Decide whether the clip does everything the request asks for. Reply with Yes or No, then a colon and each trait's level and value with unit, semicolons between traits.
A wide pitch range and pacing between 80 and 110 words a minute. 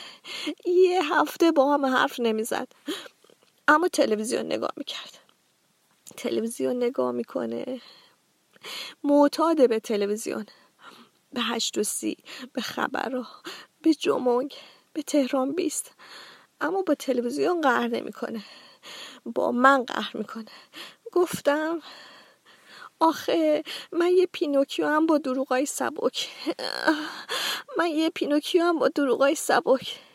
No: average, 4.6 semitones; slow, 105 wpm